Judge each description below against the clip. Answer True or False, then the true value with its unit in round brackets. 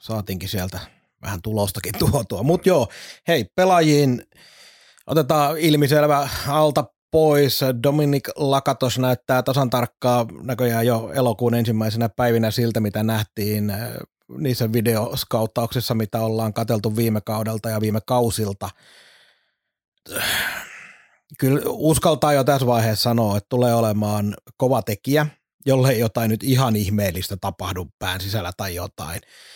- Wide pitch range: False (3.9 semitones)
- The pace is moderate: True (115 wpm)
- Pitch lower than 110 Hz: False (120 Hz)